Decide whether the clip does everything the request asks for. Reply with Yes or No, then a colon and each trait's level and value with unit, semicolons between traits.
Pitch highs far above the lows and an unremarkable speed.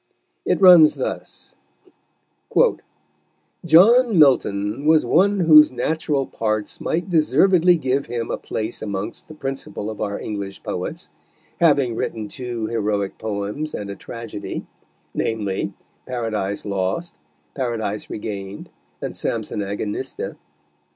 No: wide, 7.0 semitones; slow, 110 wpm